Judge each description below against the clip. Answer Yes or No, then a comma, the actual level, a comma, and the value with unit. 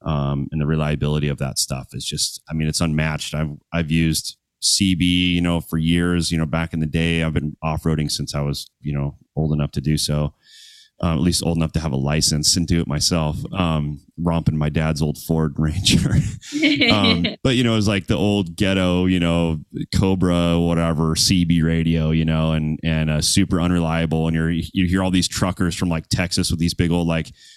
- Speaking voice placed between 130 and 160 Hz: No, very low, 80 Hz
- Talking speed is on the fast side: Yes, fast, 210 wpm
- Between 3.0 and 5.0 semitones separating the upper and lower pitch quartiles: No, narrow, 2.5 semitones